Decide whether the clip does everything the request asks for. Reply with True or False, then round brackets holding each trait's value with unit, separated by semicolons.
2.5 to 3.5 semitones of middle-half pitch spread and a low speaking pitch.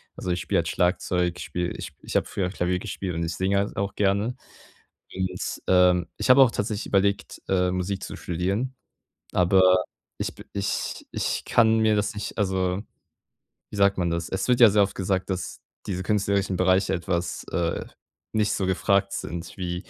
False (2.1 semitones; 95 Hz)